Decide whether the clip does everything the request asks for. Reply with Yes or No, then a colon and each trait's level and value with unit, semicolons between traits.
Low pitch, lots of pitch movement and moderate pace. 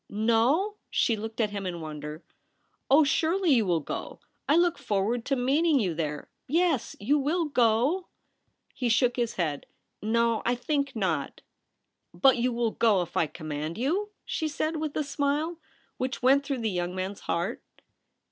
No: high, 240 Hz; wide, 7.1 semitones; average, 195 wpm